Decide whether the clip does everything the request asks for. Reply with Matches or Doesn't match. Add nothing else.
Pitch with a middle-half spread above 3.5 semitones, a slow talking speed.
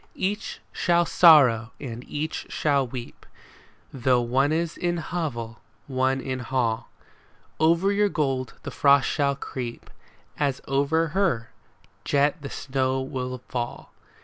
Matches